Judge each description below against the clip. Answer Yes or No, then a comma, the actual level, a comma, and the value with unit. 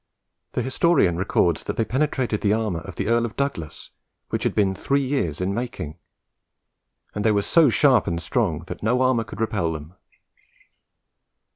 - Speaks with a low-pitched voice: Yes, low, 110 Hz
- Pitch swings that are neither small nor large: No, wide, 6.4 semitones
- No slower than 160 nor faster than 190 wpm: Yes, average, 170 wpm